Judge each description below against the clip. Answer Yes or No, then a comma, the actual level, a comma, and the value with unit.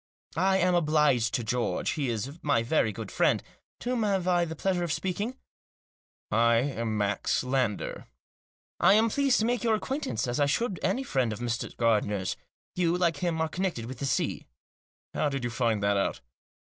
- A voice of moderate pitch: Yes, medium, 145 Hz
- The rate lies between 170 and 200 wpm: Yes, average, 195 wpm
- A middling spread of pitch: No, wide, 7.8 semitones